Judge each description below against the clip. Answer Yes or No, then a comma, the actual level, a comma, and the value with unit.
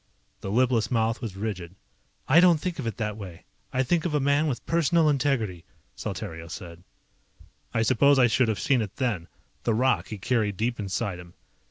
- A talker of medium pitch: No, low, 115 Hz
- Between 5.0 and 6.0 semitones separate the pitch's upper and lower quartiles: Yes, wide, 5.4 semitones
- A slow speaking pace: No, average, 190 wpm